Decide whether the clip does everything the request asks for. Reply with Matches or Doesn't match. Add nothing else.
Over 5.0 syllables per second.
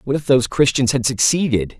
Matches